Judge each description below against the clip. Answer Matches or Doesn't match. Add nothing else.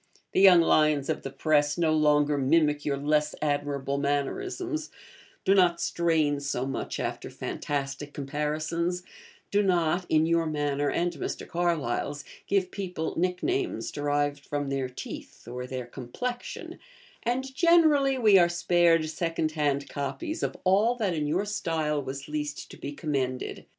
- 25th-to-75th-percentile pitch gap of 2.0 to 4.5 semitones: Matches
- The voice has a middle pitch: Matches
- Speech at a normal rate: Matches